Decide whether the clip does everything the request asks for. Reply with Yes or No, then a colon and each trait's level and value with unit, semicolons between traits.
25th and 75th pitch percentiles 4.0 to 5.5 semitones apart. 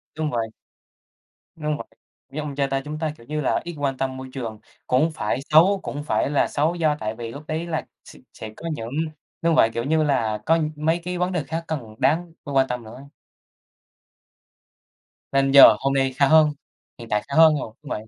No: average, 3.4 semitones